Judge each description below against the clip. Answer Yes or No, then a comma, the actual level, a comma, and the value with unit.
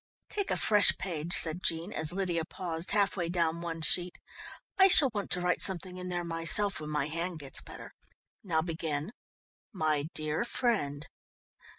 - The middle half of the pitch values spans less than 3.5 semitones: Yes, average, 2.9 semitones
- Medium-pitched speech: Yes, medium, 170 Hz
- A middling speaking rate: Yes, average, 170 wpm